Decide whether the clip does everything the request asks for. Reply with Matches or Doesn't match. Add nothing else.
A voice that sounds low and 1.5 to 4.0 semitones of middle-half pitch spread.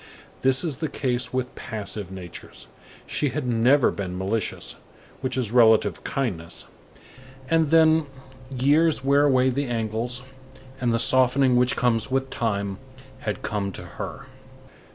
Matches